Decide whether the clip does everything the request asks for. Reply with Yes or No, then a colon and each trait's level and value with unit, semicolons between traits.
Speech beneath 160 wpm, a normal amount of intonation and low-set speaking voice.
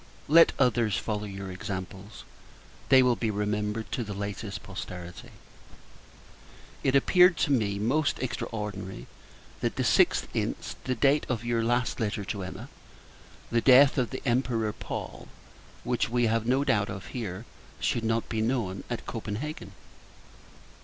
Yes: average, 145 wpm; average, 3.6 semitones; low, 115 Hz